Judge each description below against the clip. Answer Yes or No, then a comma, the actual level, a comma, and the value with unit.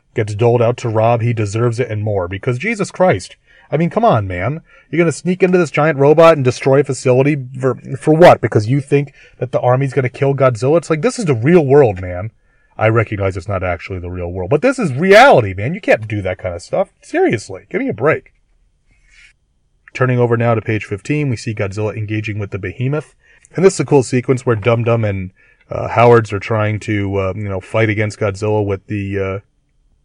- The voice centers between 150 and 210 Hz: No, low, 120 Hz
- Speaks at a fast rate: Yes, fast, 220 wpm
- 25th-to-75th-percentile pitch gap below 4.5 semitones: No, average, 5.2 semitones